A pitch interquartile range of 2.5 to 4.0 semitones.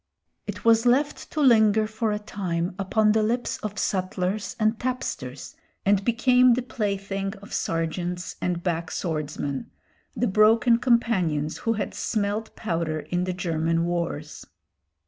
No: average, 4.7 semitones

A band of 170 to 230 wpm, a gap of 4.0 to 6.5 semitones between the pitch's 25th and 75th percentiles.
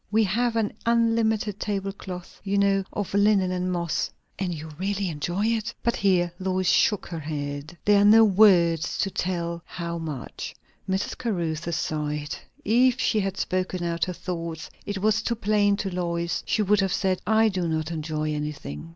No: average, 175 wpm; average, 3.6 semitones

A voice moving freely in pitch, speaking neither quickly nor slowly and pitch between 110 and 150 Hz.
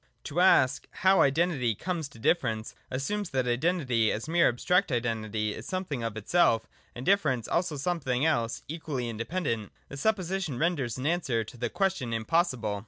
Yes: wide, 7.0 semitones; average, 170 wpm; low, 135 Hz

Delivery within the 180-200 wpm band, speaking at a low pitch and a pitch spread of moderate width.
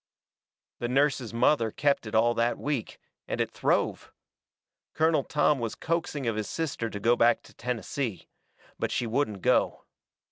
No: average, 155 wpm; low, 120 Hz; average, 4.2 semitones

